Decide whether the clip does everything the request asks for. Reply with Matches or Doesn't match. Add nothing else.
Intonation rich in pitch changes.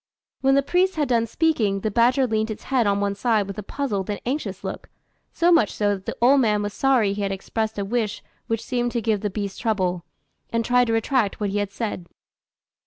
Doesn't match